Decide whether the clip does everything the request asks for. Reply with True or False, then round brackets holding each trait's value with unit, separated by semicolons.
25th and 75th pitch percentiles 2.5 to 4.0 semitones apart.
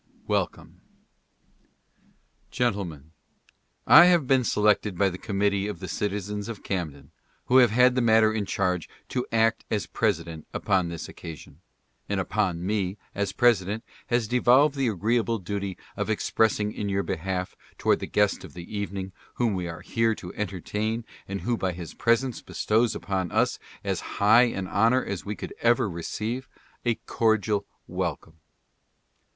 True (3.6 semitones)